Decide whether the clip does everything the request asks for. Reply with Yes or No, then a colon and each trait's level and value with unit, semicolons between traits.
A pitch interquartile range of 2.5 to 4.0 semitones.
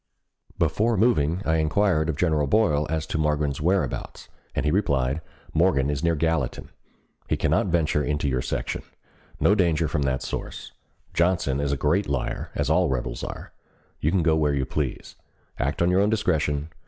Yes: average, 3.3 semitones